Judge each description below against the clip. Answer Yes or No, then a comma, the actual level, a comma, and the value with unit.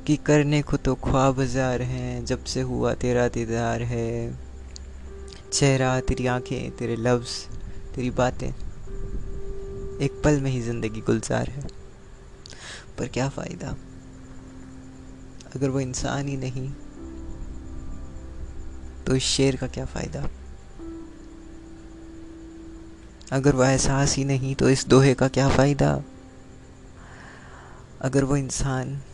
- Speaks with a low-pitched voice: Yes, low, 125 Hz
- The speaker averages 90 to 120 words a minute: Yes, slow, 110 wpm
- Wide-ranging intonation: Yes, wide, 5.7 semitones